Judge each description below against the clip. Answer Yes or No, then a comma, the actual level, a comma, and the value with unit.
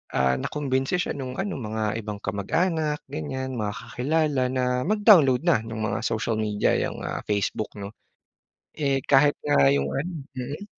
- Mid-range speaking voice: No, low, 130 Hz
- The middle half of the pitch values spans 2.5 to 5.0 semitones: No, wide, 5.6 semitones